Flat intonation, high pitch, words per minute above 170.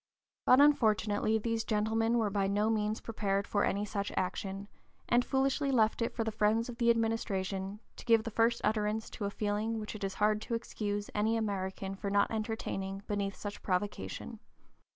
Yes: narrow, 2.0 semitones; high, 215 Hz; average, 180 wpm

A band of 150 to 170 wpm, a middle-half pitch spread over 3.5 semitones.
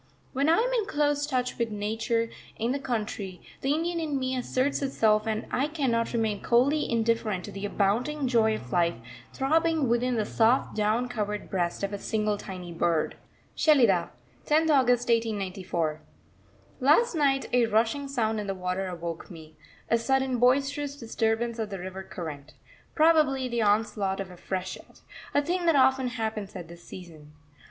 Yes: average, 165 wpm; wide, 5.4 semitones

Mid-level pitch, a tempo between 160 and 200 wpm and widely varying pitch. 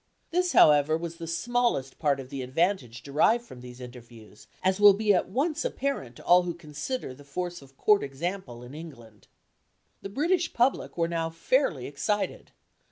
Yes: medium, 165 Hz; average, 170 wpm; wide, 7.4 semitones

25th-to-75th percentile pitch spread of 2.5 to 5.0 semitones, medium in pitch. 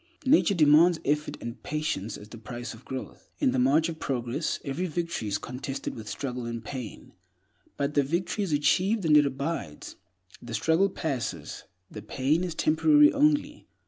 No: wide, 5.5 semitones; medium, 145 Hz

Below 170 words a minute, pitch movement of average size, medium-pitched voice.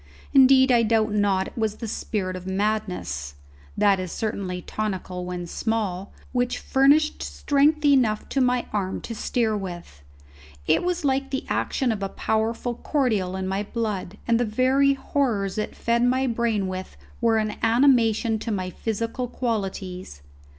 No: average, 155 wpm; average, 4.5 semitones; high, 220 Hz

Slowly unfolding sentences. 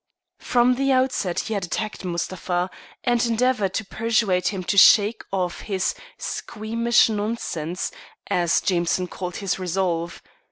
Yes: slow, 130 wpm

